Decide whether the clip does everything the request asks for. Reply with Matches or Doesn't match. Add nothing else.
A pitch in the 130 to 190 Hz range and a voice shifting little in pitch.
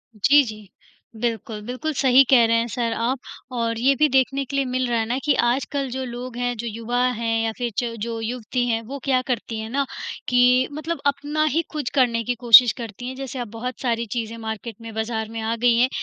Doesn't match